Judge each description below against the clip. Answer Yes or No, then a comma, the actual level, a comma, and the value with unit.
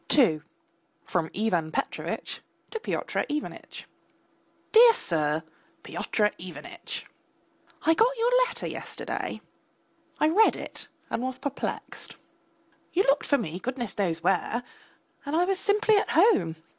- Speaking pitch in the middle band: No, very high, 265 Hz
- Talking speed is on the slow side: Yes, slow, 125 wpm